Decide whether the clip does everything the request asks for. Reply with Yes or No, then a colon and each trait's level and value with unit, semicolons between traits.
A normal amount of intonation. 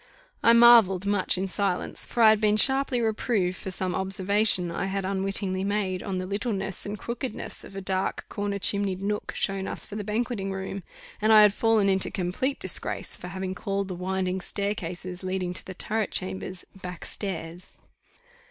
No: narrow, 2.1 semitones